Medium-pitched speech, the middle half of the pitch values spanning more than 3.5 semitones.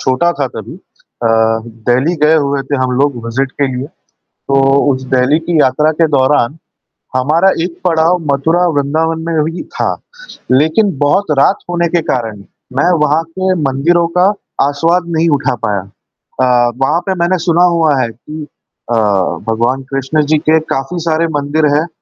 Yes: medium, 150 Hz; average, 4.0 semitones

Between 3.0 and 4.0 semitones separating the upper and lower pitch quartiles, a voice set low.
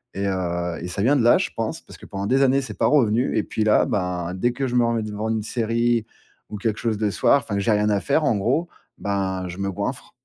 Yes: average, 3.5 semitones; low, 110 Hz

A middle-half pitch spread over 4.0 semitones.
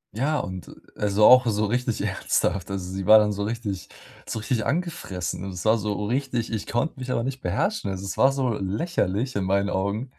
Yes: average, 4.4 semitones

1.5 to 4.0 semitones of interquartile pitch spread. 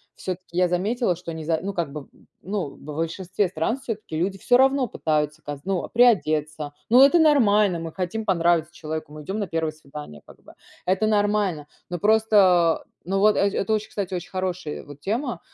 No: average, 4.8 semitones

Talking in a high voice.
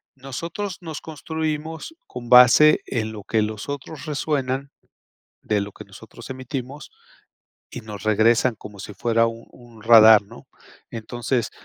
No: low, 120 Hz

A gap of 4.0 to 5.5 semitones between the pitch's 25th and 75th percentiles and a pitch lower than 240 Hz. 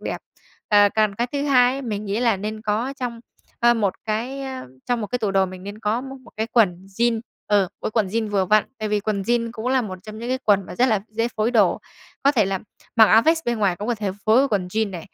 No: average, 2.8 semitones; high, 220 Hz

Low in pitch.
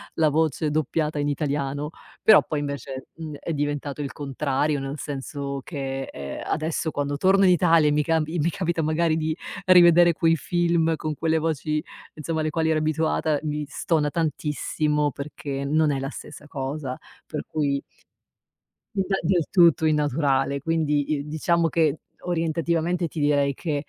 No: medium, 155 Hz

